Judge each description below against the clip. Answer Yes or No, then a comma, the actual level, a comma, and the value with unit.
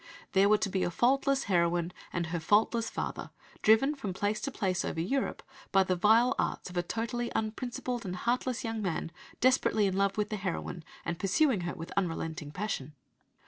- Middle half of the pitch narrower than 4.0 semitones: No, average, 4.8 semitones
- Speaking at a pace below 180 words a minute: No, average, 185 wpm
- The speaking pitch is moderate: No, high, 200 Hz